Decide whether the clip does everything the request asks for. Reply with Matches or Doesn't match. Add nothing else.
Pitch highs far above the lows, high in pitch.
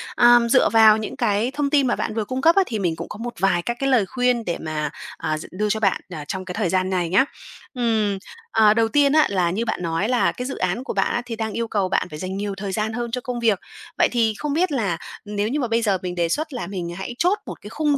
Doesn't match